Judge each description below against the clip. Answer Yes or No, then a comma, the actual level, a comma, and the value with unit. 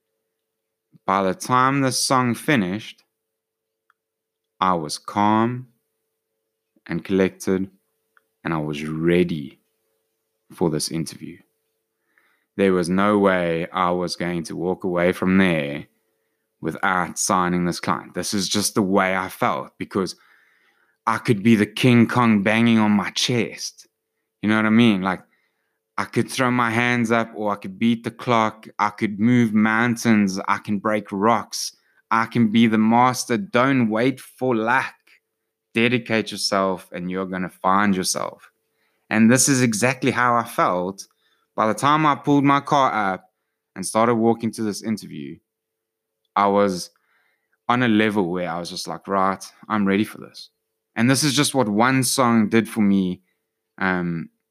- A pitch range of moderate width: Yes, average, 3.3 semitones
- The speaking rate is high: No, average, 155 wpm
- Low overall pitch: Yes, low, 110 Hz